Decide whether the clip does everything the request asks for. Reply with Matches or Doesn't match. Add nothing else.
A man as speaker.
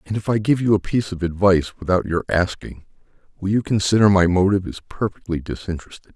Matches